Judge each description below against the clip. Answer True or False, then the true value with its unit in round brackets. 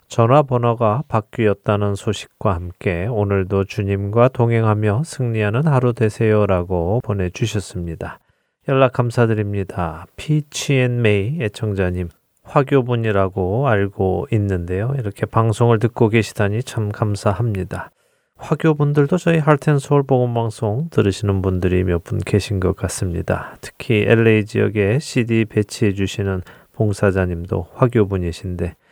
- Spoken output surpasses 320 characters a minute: False (305 characters per minute)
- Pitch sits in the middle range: False (105 Hz)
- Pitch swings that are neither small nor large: True (4.0 semitones)